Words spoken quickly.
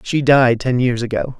Yes: fast, 215 wpm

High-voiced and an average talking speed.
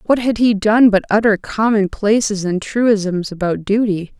Yes: high, 210 Hz; average, 170 wpm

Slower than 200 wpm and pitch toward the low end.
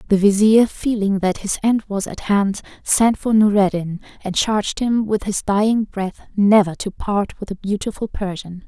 No: average, 180 wpm; high, 205 Hz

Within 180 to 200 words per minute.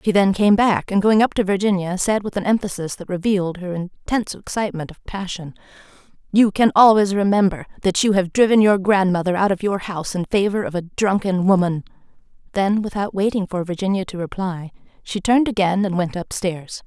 Yes: average, 190 wpm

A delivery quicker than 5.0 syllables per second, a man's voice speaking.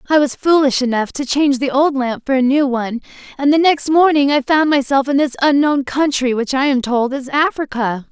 No: 5.4 syllables/s; female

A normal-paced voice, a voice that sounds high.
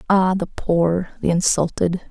No: average, 145 wpm; medium, 180 Hz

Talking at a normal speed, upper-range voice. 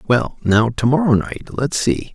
No: average, 195 wpm; low, 130 Hz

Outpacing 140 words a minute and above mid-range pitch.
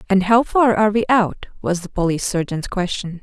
Yes: fast, 205 wpm; high, 200 Hz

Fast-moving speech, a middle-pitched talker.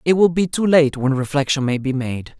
Yes: fast, 250 wpm; medium, 145 Hz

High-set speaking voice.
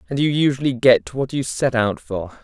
No: low, 125 Hz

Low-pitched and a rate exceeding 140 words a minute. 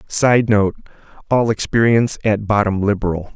No: low, 105 Hz; slow, 105 wpm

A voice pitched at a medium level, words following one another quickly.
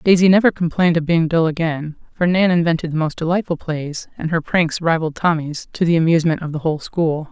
Yes: medium, 165 Hz; fast, 215 wpm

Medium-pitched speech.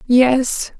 No: very high, 255 Hz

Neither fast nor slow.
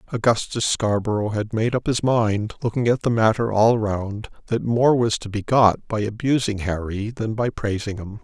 Yes: average, 190 wpm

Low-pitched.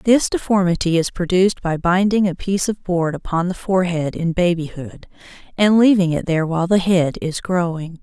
No: medium, 180 Hz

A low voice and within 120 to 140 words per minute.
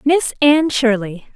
No: very high, 260 Hz; slow, 135 wpm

